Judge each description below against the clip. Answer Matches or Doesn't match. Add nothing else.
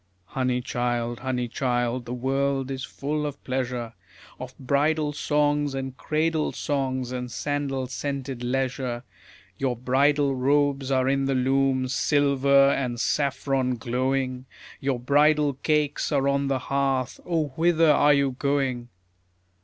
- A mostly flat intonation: Matches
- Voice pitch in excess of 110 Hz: Matches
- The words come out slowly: Matches